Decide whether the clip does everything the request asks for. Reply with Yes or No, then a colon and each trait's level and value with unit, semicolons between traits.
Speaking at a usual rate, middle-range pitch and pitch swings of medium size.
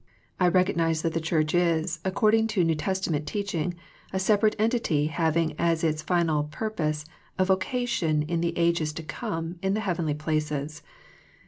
Yes: average, 155 wpm; medium, 170 Hz; average, 3.3 semitones